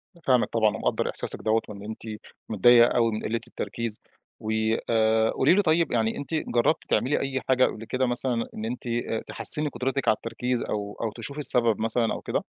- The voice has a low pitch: Yes, low, 120 Hz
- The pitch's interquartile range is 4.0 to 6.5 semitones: No, average, 2.9 semitones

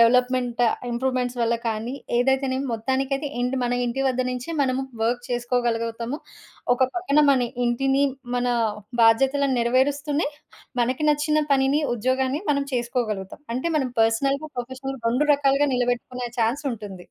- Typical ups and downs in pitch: No, narrow, 2.3 semitones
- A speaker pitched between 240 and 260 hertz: Yes, very high, 255 Hz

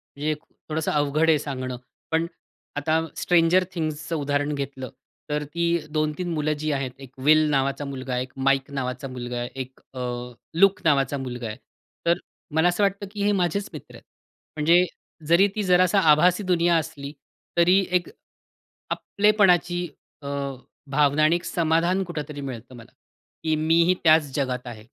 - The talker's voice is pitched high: No, medium, 155 Hz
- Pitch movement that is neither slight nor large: Yes, average, 4.0 semitones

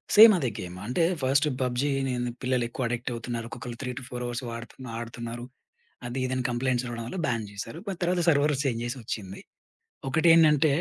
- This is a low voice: Yes, low, 125 Hz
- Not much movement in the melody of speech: No, average, 3.2 semitones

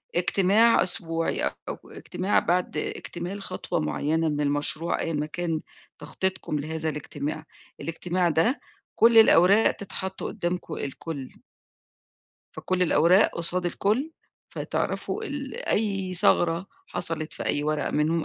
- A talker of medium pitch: Yes, medium, 175 Hz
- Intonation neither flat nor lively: Yes, average, 3.2 semitones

